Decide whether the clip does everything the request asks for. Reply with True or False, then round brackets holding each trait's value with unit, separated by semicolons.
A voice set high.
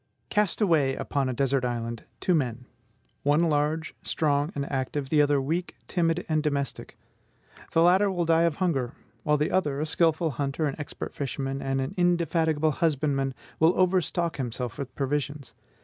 False (150 Hz)